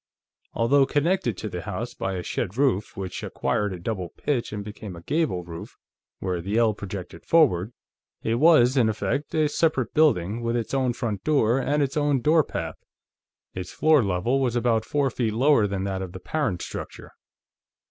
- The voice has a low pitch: Yes, low, 115 Hz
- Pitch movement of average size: No, wide, 6.5 semitones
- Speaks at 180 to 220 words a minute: Yes, average, 185 wpm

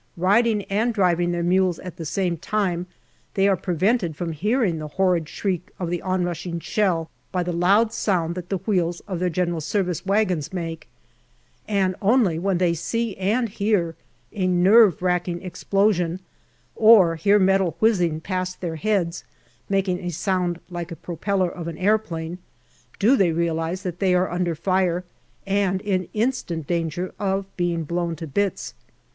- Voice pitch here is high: No, medium, 180 Hz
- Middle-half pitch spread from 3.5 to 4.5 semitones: No, narrow, 2.5 semitones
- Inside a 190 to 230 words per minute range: No, average, 165 wpm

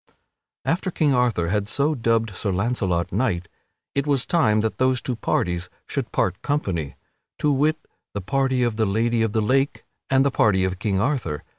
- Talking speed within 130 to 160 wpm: No, average, 180 wpm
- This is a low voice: Yes, low, 115 Hz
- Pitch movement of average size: No, wide, 5.7 semitones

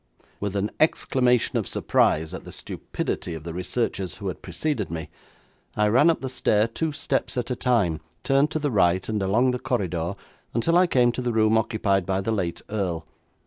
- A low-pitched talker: Yes, low, 110 Hz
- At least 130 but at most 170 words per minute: No, average, 195 wpm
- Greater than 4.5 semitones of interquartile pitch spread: Yes, average, 5.1 semitones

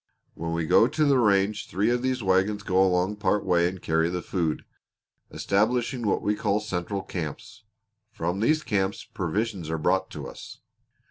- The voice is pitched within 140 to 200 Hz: No, low, 100 Hz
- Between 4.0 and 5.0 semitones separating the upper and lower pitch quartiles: No, average, 3.5 semitones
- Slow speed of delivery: No, average, 175 wpm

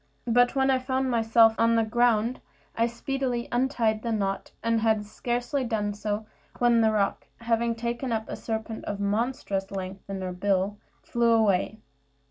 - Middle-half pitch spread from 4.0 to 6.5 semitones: No, narrow, 2.5 semitones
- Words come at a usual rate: Yes, average, 165 wpm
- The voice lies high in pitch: Yes, high, 225 Hz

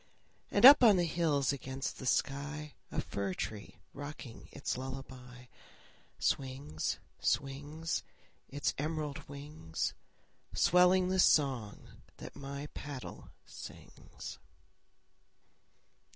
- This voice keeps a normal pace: No, slow, 95 wpm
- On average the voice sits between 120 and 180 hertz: Yes, medium, 140 Hz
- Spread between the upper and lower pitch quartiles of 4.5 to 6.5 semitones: No, average, 2.8 semitones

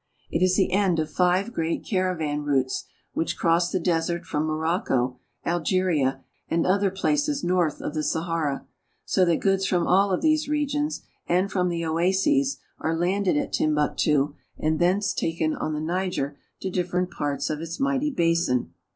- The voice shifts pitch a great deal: No, average, 3.4 semitones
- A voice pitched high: No, medium, 175 Hz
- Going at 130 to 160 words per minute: No, average, 170 wpm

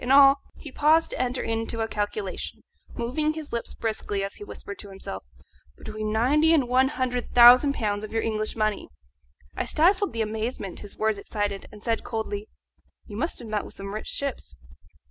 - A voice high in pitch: Yes, high, 225 Hz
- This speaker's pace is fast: No, average, 190 wpm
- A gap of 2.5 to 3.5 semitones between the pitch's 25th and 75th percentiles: No, average, 3.9 semitones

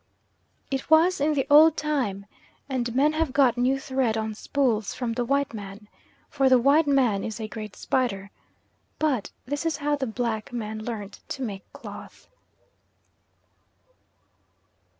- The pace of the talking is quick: No, average, 150 wpm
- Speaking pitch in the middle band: No, very high, 255 Hz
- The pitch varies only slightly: No, average, 4.5 semitones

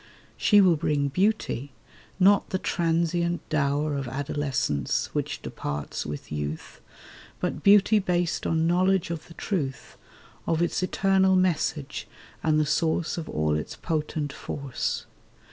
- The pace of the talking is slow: Yes, slow, 130 wpm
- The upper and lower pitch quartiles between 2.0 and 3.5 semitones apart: No, average, 4.5 semitones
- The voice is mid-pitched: Yes, medium, 160 Hz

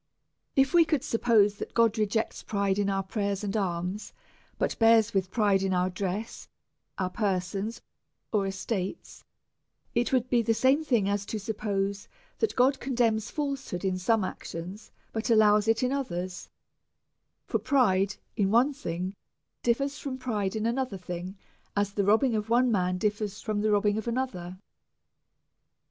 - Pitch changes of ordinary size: Yes, average, 3.4 semitones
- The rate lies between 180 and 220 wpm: No, average, 160 wpm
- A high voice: Yes, high, 210 Hz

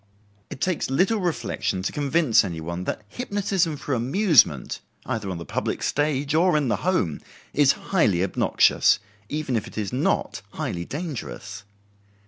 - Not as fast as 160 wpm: Yes, average, 150 wpm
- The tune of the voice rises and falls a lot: Yes, wide, 8.9 semitones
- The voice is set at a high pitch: No, medium, 140 Hz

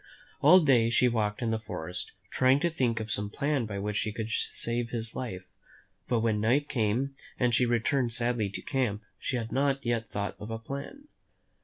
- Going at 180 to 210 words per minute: Yes, average, 195 wpm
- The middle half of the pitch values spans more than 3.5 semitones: No, average, 3.2 semitones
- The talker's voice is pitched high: No, low, 115 Hz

